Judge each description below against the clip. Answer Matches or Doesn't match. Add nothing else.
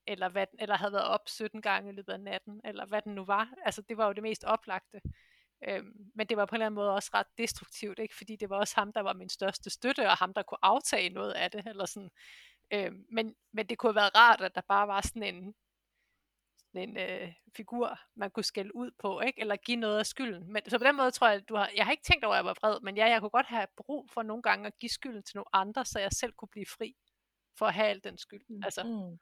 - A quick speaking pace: Matches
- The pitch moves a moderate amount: Doesn't match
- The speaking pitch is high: Matches